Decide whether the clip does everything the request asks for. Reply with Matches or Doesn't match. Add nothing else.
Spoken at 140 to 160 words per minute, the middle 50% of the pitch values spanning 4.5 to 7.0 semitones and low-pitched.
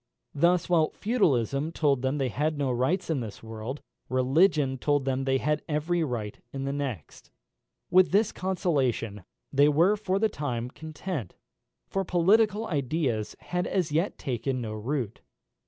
Doesn't match